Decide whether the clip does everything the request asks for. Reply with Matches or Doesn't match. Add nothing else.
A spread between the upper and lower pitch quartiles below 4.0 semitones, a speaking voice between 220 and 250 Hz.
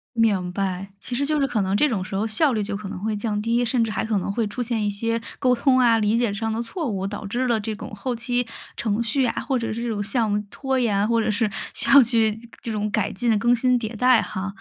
Matches